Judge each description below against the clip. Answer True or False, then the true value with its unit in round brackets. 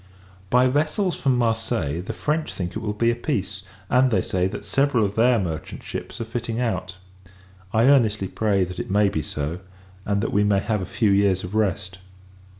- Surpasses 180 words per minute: True (200 wpm)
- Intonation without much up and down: False (4.0 semitones)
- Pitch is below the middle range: True (105 Hz)